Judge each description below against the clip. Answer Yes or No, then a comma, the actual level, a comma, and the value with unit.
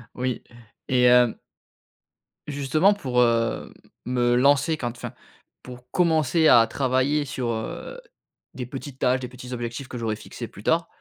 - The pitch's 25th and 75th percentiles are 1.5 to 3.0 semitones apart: Yes, narrow, 2.6 semitones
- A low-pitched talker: Yes, low, 125 Hz